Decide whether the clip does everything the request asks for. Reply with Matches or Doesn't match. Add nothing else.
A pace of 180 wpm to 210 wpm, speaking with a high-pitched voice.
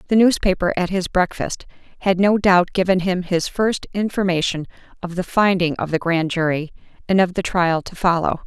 Doesn't match